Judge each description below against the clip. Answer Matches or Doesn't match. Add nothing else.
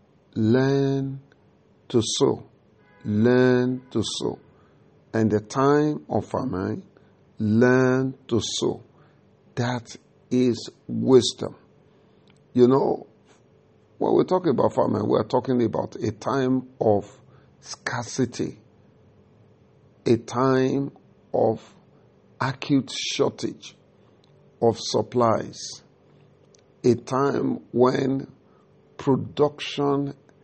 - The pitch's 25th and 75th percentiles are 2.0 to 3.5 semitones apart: Matches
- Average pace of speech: Doesn't match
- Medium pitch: Doesn't match